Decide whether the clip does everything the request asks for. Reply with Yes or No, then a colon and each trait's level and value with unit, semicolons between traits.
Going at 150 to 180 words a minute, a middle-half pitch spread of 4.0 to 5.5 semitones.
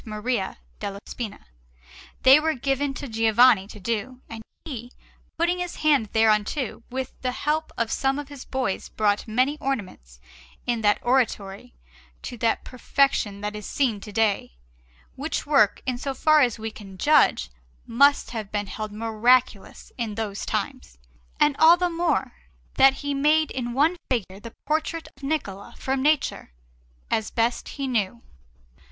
Yes: average, 155 wpm; average, 4.8 semitones